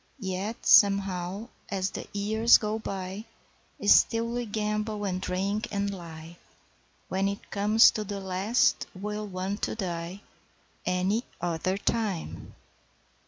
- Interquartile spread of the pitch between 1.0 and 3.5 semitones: Yes, narrow, 2.4 semitones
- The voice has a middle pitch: No, high, 200 Hz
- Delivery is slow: Yes, slow, 120 wpm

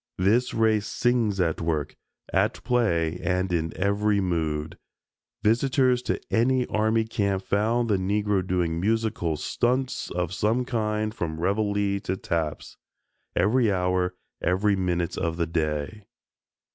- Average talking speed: No, slow, 130 wpm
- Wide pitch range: No, average, 4.2 semitones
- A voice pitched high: No, low, 100 Hz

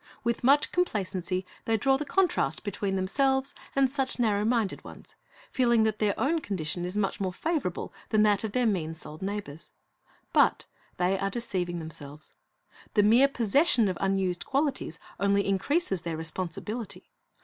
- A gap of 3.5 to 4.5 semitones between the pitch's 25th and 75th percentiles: No, average, 5.3 semitones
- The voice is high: Yes, high, 205 Hz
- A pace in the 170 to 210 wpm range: No, average, 155 wpm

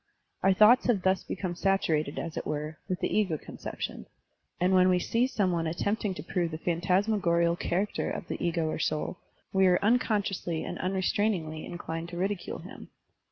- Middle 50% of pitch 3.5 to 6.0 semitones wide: No, average, 2.7 semitones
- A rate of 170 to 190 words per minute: Yes, average, 180 wpm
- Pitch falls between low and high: Yes, medium, 180 Hz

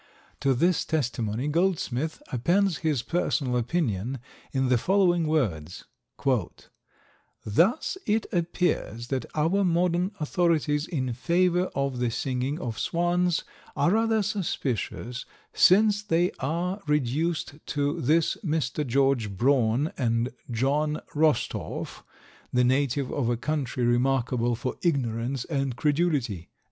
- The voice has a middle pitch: Yes, medium, 145 Hz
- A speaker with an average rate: No, slow, 115 wpm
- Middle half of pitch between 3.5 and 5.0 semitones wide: No, wide, 5.6 semitones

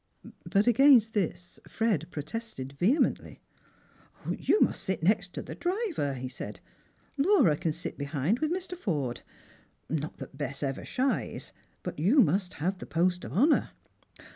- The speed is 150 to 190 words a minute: No, average, 140 wpm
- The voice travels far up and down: Yes, wide, 8.6 semitones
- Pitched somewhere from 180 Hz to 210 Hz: Yes, medium, 185 Hz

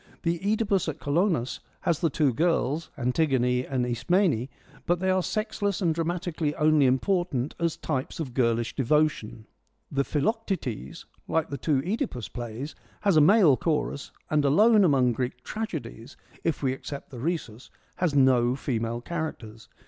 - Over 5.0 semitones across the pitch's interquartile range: Yes, wide, 5.5 semitones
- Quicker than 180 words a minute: No, average, 150 wpm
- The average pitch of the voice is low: No, medium, 150 Hz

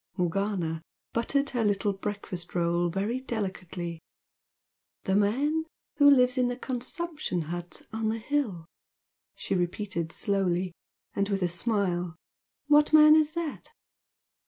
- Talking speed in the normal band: No, slow, 125 wpm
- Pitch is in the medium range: No, high, 205 Hz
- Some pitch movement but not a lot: No, wide, 6.5 semitones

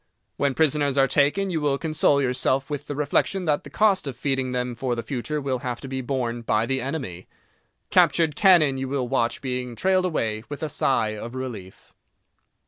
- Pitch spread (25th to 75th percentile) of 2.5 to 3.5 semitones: Yes, average, 3.1 semitones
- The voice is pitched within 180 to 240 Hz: No, low, 135 Hz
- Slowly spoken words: No, average, 195 wpm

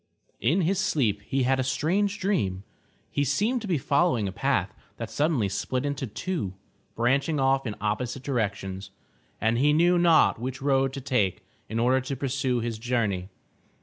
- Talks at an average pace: Yes, average, 170 wpm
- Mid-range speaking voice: No, low, 130 Hz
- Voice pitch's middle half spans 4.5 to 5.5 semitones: Yes, average, 4.8 semitones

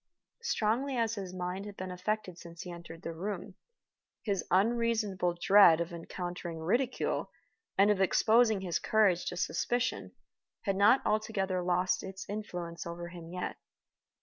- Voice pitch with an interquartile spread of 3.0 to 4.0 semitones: Yes, average, 3.4 semitones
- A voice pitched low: No, high, 190 Hz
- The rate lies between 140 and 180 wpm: Yes, average, 150 wpm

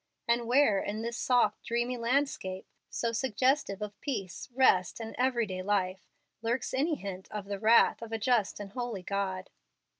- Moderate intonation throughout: Yes, average, 3.7 semitones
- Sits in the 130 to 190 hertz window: No, high, 225 Hz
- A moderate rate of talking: Yes, average, 160 wpm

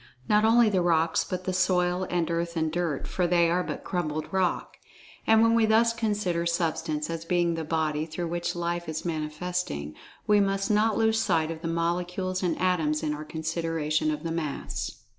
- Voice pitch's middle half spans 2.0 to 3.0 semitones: Yes, narrow, 2.5 semitones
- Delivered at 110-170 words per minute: No, average, 190 wpm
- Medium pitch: Yes, medium, 170 Hz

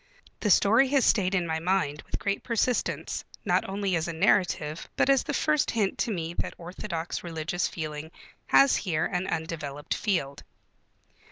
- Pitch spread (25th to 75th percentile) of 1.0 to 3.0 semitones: No, average, 4.4 semitones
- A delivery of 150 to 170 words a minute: Yes, average, 165 wpm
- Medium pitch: Yes, medium, 180 Hz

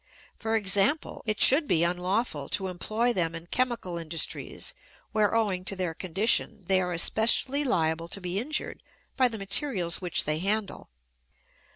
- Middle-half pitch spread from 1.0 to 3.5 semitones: No, average, 4.6 semitones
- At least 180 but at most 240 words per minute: No, average, 155 wpm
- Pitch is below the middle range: No, high, 195 Hz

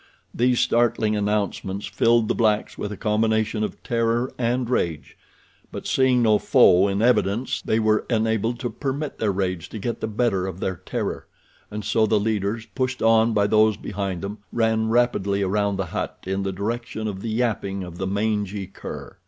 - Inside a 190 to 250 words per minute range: No, average, 180 wpm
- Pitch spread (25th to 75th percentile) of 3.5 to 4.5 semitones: No, average, 2.7 semitones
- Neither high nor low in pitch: No, low, 110 Hz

